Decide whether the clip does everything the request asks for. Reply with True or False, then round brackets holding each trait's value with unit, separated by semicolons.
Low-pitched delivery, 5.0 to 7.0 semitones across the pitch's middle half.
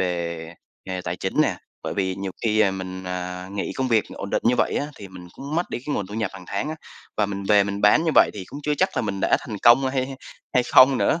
True (100 Hz; 5.5 semitones)